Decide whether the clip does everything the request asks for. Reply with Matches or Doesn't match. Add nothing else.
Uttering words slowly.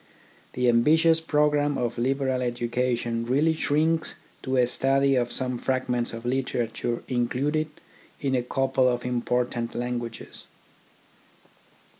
Matches